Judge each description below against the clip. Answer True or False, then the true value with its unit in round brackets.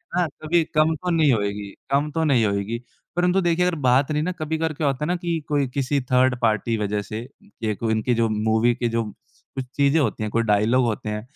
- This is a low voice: True (130 Hz)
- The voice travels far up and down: True (5.9 semitones)